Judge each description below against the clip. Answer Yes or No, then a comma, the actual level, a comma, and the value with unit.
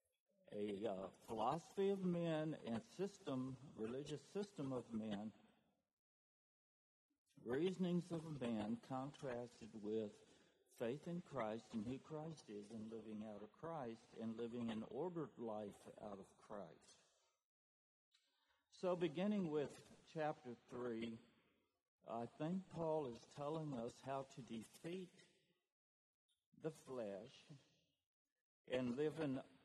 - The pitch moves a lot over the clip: Yes, wide, 6.2 semitones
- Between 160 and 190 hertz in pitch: No, low, 135 Hz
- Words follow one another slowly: Yes, slow, 110 wpm